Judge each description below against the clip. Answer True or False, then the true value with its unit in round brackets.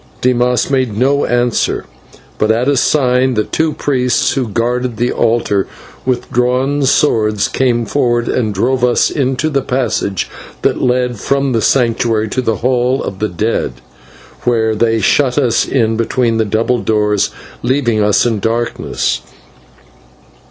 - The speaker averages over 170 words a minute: False (145 wpm)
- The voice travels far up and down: False (2.5 semitones)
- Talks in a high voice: False (120 Hz)